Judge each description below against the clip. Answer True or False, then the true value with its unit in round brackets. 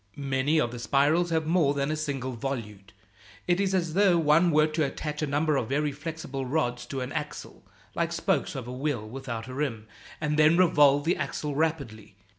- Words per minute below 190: False (200 wpm)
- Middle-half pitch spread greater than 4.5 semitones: False (3.3 semitones)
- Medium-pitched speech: True (145 Hz)